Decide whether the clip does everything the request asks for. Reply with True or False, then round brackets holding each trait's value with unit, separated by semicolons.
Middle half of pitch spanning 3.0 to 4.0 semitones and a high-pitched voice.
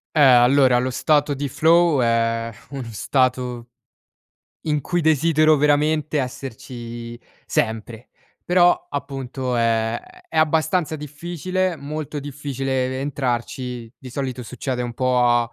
False (3.6 semitones; 135 Hz)